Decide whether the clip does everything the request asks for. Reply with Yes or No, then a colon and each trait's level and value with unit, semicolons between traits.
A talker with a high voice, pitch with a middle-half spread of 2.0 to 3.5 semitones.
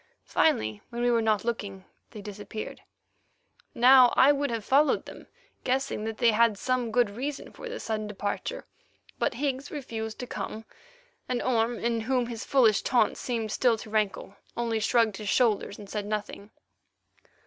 Yes: high, 230 Hz; average, 2.7 semitones